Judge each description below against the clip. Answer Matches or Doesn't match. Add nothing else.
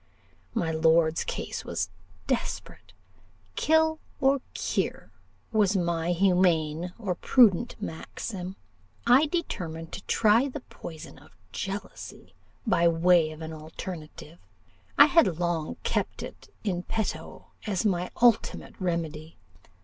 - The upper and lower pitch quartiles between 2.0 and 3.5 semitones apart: Doesn't match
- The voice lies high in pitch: Doesn't match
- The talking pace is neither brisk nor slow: Doesn't match